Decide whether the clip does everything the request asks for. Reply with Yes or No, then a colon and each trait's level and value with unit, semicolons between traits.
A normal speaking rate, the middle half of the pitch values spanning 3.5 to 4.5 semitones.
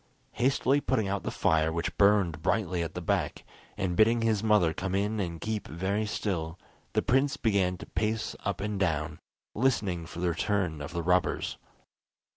Yes: average, 175 wpm; average, 4.2 semitones